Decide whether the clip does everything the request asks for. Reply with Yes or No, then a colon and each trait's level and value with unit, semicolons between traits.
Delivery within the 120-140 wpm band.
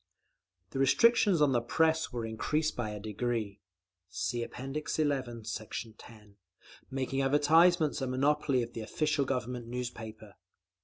Yes: slow, 135 wpm